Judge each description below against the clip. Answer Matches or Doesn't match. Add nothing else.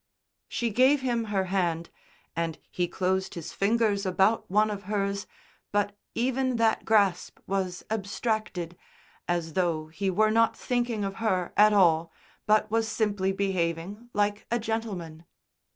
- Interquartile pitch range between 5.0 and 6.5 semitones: Doesn't match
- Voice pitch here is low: Doesn't match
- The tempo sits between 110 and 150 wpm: Matches